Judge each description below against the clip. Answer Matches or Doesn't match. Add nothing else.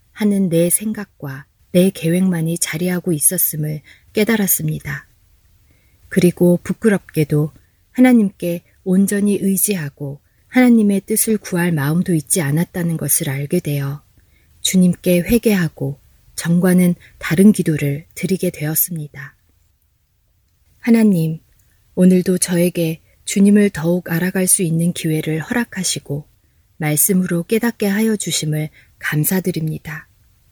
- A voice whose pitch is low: Doesn't match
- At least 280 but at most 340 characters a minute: Doesn't match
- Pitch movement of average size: Matches